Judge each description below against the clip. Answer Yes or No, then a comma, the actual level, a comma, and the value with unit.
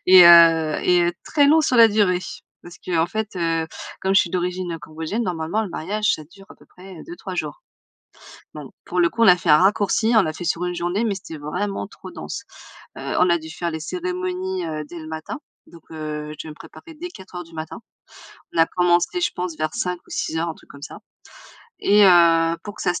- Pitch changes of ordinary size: Yes, average, 3.0 semitones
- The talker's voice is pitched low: No, medium, 175 Hz